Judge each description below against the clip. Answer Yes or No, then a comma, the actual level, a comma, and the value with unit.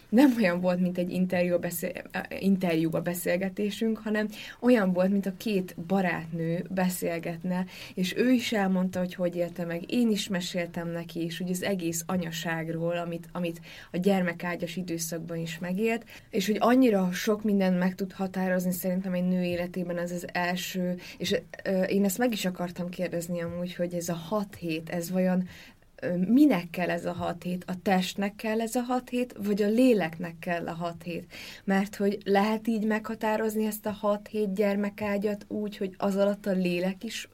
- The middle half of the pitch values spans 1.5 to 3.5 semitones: Yes, average, 2.9 semitones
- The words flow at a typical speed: No, fast, 175 wpm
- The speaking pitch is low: No, medium, 185 Hz